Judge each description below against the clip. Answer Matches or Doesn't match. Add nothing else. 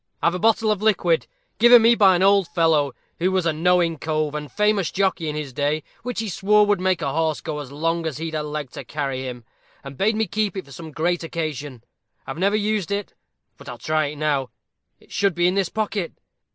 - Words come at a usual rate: Doesn't match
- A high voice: Doesn't match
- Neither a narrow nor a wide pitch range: Matches